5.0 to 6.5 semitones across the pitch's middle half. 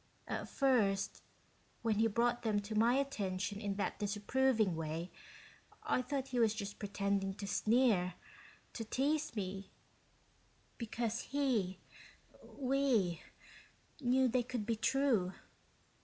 No: average, 4.3 semitones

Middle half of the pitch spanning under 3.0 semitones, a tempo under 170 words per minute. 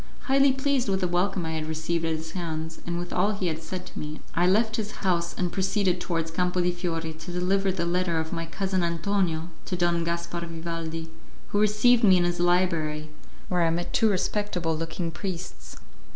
No: narrow, 2.6 semitones; average, 200 wpm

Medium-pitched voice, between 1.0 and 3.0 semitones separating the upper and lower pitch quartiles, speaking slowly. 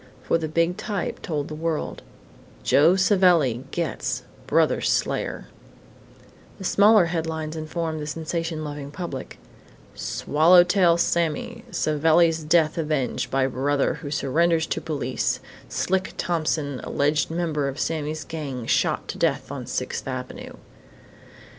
Yes: medium, 160 Hz; narrow, 2.6 semitones; slow, 125 wpm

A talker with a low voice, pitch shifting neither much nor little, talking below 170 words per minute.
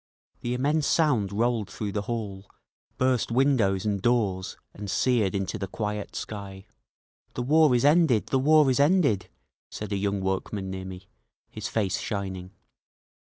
Yes: low, 105 Hz; average, 4.7 semitones; average, 155 wpm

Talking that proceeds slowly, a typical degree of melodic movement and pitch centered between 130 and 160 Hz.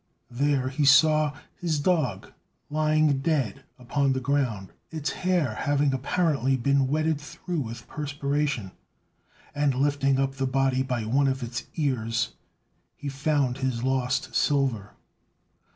No: slow, 130 wpm; narrow, 2.3 semitones; low, 135 Hz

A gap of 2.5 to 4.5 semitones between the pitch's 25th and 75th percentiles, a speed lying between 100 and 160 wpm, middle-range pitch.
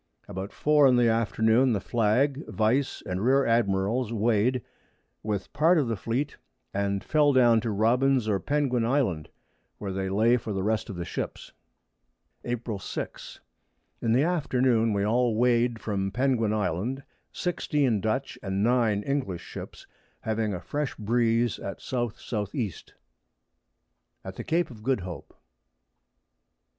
No: average, 3.8 semitones; average, 150 wpm; low, 115 Hz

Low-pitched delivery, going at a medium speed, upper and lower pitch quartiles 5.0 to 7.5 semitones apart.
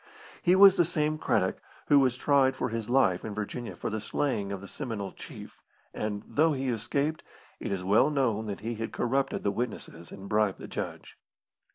Yes: low, 120 Hz; average, 195 wpm; average, 5.3 semitones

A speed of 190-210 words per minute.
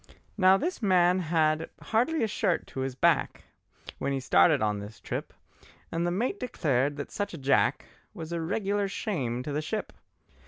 No: average, 180 wpm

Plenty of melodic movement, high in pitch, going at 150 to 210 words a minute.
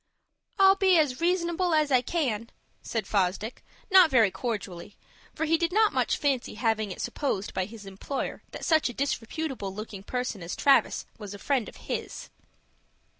Yes: wide, 7.5 semitones; very high, 250 Hz; average, 170 wpm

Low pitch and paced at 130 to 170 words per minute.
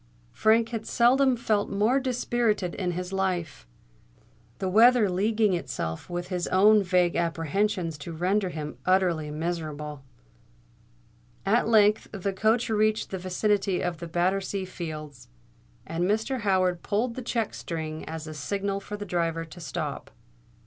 No: high, 190 Hz; average, 140 wpm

